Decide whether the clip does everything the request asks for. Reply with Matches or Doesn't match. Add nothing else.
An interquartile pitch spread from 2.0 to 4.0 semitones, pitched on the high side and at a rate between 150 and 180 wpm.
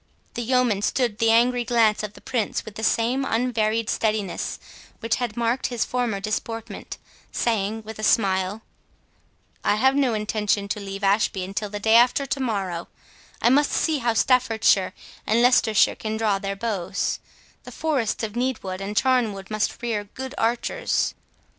Matches